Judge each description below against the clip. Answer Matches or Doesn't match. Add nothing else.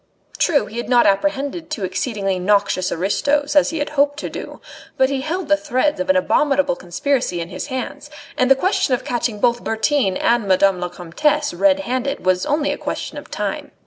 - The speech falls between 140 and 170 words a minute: Doesn't match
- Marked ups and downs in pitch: Matches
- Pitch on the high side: Matches